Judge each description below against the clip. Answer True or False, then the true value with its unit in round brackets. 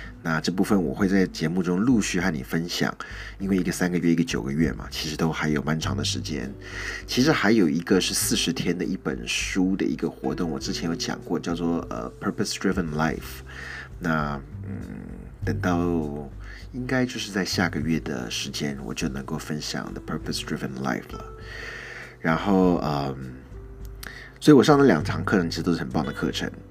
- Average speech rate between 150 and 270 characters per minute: False (340 characters per minute)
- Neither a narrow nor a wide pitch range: True (4.3 semitones)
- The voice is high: False (85 Hz)